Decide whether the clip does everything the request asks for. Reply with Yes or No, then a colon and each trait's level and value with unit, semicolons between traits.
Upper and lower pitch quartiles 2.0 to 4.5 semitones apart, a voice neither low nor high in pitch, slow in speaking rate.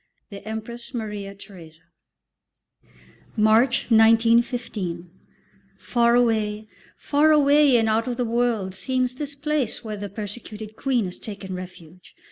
No: average, 3.3 semitones; high, 225 Hz; slow, 120 wpm